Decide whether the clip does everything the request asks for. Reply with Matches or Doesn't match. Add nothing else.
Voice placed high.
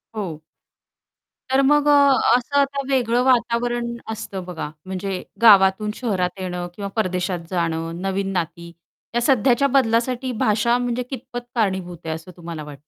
Matches